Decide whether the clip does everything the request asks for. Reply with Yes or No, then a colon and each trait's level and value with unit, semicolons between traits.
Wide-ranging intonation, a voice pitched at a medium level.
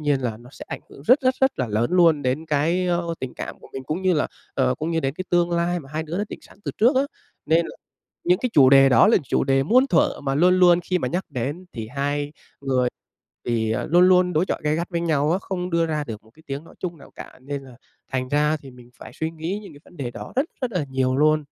No: average, 4.7 semitones; medium, 155 Hz